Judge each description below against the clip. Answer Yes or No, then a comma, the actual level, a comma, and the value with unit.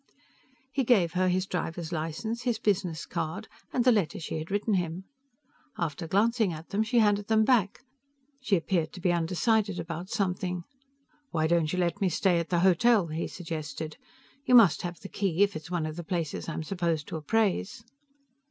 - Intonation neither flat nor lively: Yes, average, 4.0 semitones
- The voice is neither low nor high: Yes, medium, 180 Hz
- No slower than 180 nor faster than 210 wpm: Yes, average, 185 wpm